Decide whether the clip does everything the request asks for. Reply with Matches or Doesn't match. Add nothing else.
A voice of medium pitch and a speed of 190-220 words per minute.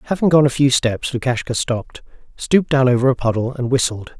Doesn't match